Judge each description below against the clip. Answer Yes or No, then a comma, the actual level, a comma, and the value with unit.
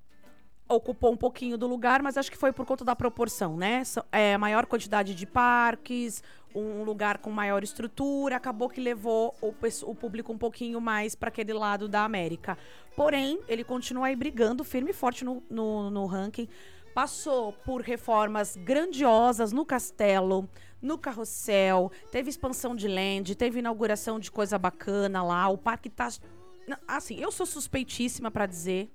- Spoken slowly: No, average, 160 wpm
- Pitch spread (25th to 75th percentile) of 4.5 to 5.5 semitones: No, average, 3.4 semitones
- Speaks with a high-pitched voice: Yes, high, 230 Hz